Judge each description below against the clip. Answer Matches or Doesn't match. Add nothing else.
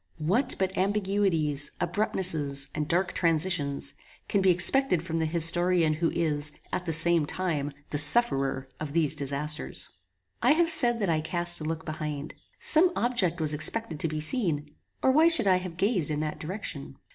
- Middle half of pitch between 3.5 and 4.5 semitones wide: Matches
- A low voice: Doesn't match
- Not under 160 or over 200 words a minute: Matches